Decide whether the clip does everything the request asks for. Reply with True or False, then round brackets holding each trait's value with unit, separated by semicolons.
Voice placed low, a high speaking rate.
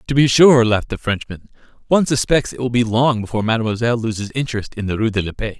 True (115 Hz; 235 wpm)